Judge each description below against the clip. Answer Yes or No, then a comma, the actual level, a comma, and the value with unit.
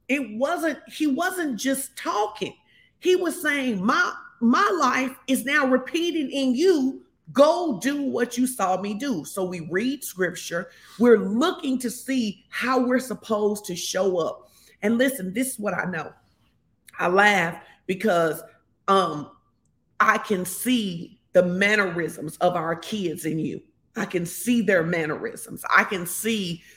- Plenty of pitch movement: Yes, wide, 6.0 semitones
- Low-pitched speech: No, high, 225 Hz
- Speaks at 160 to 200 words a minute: No, average, 150 wpm